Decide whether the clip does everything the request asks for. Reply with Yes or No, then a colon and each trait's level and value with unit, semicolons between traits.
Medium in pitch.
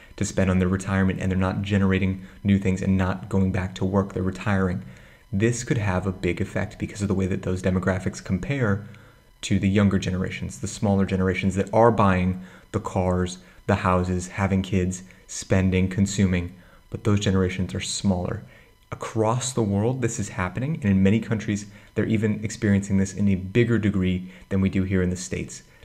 No: very low, 95 Hz